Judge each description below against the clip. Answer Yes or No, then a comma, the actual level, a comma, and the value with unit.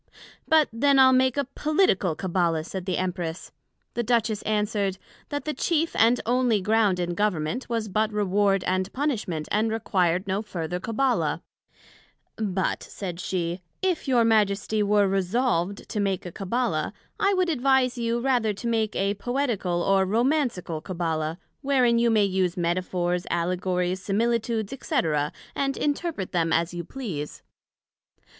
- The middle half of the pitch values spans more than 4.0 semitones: Yes, average, 5.1 semitones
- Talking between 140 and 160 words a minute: Yes, average, 145 wpm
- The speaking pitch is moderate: No, high, 205 Hz